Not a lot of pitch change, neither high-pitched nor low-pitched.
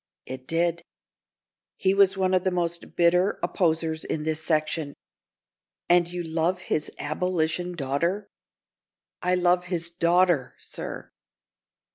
Yes: narrow, 2.2 semitones; medium, 170 Hz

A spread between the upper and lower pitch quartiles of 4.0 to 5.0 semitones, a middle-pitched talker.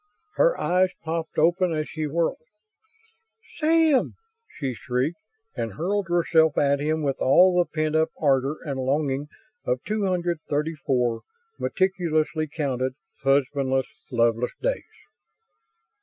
Yes: average, 4.3 semitones; medium, 155 Hz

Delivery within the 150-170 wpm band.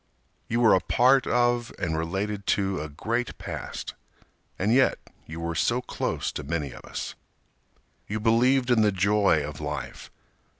Yes: average, 160 wpm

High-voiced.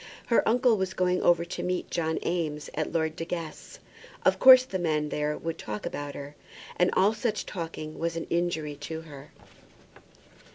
No: medium, 165 Hz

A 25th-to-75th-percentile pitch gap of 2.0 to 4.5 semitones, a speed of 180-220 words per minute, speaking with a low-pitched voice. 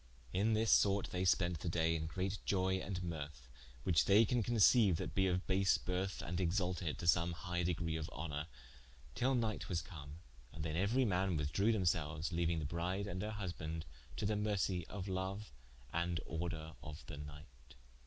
Yes: average, 3.3 semitones; average, 185 wpm; very low, 90 Hz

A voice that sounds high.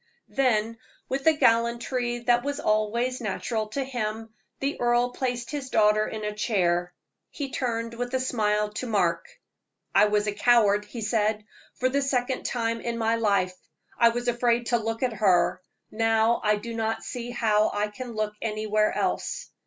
Yes: high, 230 Hz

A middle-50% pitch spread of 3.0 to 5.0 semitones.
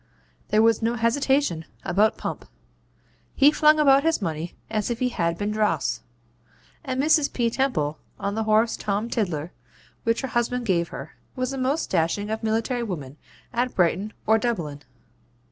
No: wide, 5.4 semitones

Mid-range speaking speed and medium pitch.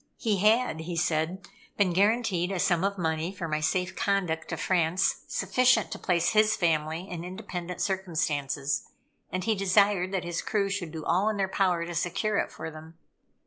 Yes: average, 185 wpm; medium, 180 Hz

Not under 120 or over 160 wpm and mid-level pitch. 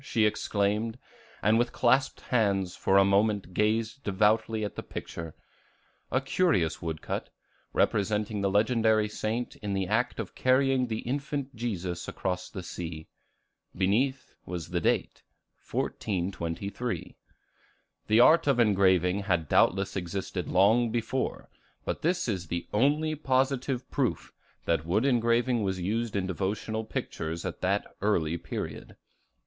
No: slow, 135 wpm; low, 105 Hz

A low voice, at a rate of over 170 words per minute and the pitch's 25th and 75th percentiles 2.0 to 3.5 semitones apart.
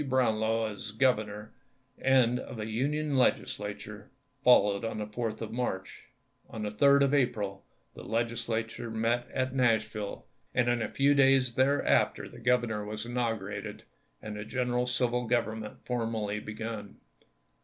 No: low, 115 Hz; average, 145 wpm; narrow, 2.6 semitones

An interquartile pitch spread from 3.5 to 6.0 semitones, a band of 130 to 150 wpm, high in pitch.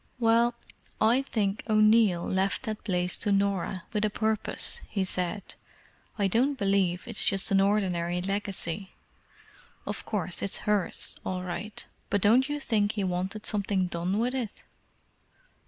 No: average, 2.7 semitones; average, 145 wpm; high, 200 Hz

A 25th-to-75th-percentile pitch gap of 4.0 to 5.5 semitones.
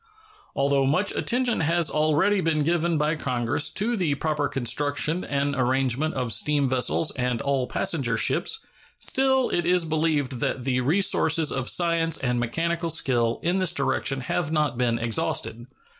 Yes: average, 4.5 semitones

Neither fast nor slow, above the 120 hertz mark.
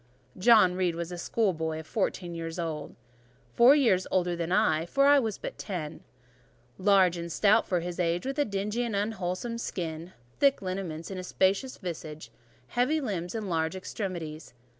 Yes: average, 170 wpm; medium, 185 Hz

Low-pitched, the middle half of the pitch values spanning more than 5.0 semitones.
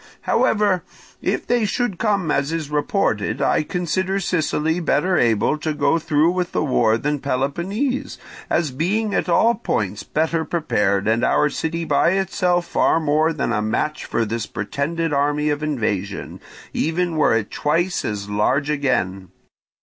No: medium, 155 Hz; wide, 5.5 semitones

